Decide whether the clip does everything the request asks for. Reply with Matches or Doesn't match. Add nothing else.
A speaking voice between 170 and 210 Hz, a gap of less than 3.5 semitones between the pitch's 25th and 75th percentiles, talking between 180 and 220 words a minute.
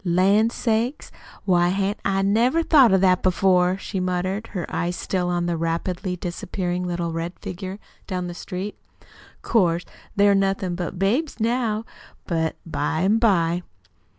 Doesn't match